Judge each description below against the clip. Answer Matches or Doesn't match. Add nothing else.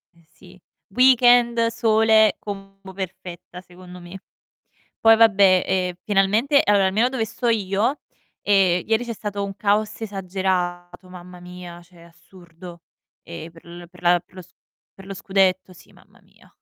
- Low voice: Doesn't match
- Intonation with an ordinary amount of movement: Matches